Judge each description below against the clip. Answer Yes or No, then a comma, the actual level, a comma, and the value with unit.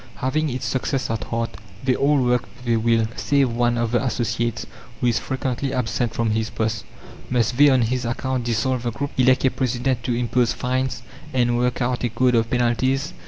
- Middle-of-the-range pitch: No, low, 125 Hz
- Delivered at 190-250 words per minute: Yes, average, 200 wpm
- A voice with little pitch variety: Yes, narrow, 1.8 semitones